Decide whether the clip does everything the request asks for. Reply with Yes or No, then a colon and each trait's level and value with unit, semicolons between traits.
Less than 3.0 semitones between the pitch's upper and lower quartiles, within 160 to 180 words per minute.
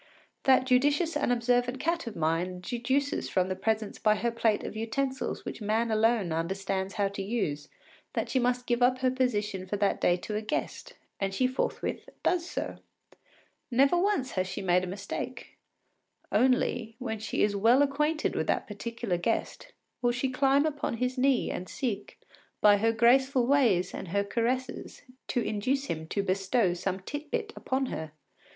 No: average, 4.8 semitones; average, 175 wpm